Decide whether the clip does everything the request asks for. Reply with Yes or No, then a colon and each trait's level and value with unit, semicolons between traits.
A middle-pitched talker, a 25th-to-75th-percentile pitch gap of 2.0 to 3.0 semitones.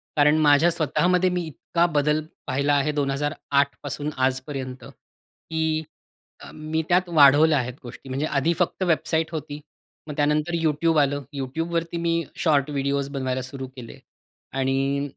Yes: medium, 145 Hz; narrow, 2.6 semitones